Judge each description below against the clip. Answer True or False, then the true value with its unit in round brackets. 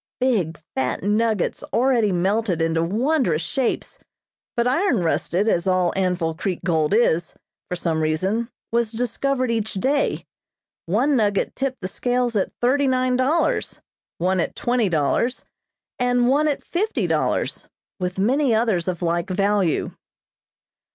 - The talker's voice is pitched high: True (210 Hz)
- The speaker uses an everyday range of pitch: False (6.0 semitones)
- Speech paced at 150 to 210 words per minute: False (135 wpm)